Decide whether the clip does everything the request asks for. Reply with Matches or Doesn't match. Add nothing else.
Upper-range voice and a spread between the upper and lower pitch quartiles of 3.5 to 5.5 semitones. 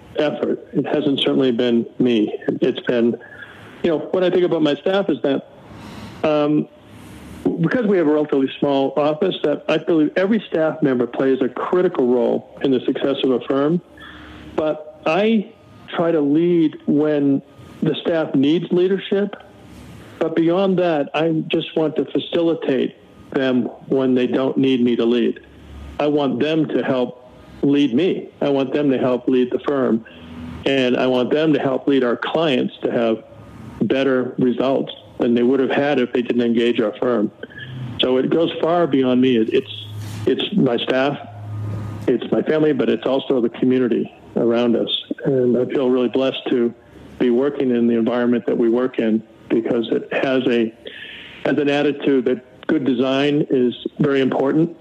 Doesn't match